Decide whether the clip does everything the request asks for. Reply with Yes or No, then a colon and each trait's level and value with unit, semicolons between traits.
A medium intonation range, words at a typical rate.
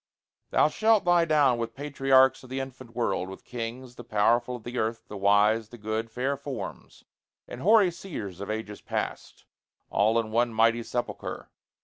Yes: average, 3.3 semitones; average, 170 wpm